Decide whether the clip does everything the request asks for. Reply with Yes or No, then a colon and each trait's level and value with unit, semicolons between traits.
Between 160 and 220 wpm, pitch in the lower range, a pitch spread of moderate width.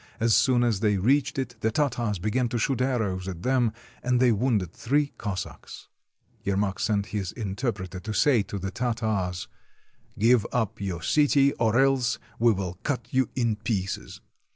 Yes: average, 175 wpm; low, 110 Hz; average, 4.1 semitones